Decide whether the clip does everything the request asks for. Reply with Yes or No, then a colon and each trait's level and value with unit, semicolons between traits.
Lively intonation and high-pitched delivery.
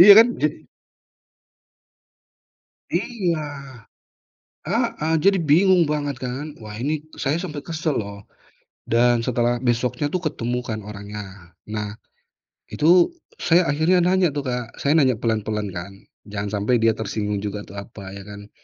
No: wide, 6.7 semitones; low, 125 Hz